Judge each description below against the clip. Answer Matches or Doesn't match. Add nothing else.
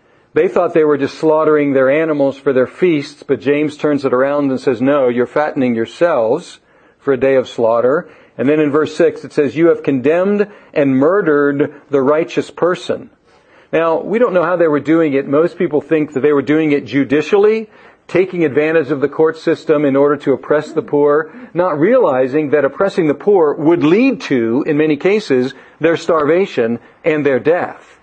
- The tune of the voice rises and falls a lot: Doesn't match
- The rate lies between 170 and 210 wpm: Matches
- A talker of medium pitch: Matches